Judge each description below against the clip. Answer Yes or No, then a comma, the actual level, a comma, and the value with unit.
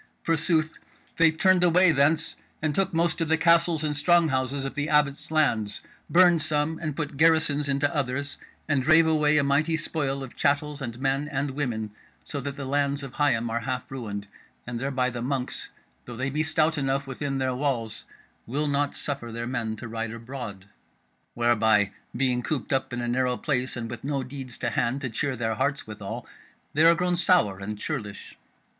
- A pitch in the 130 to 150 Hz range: Yes, medium, 140 Hz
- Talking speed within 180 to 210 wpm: Yes, average, 190 wpm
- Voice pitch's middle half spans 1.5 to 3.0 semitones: No, average, 3.9 semitones